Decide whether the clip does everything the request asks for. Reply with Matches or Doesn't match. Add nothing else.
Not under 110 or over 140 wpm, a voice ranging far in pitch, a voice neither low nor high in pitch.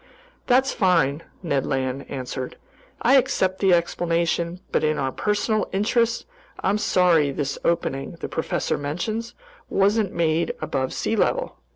Matches